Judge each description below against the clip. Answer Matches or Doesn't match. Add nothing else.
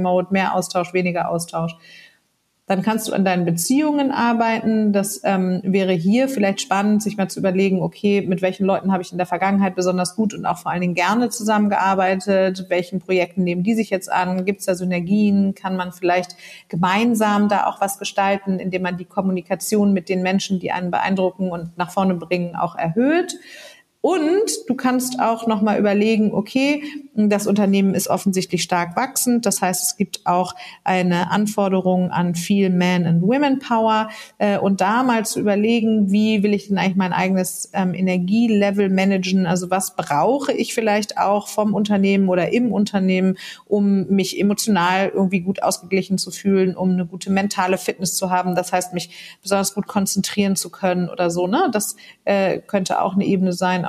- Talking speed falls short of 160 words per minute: Doesn't match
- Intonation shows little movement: Matches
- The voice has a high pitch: Matches